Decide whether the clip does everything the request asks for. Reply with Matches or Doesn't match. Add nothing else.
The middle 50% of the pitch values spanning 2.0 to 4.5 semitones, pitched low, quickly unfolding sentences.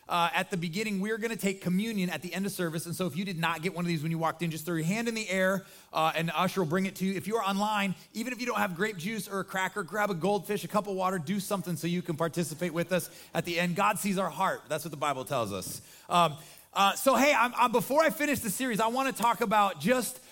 Doesn't match